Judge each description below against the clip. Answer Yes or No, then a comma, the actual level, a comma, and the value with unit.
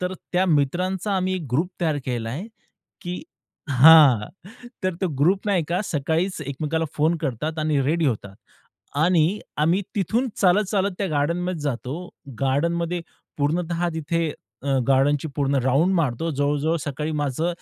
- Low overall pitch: No, medium, 160 Hz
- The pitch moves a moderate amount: Yes, average, 3.8 semitones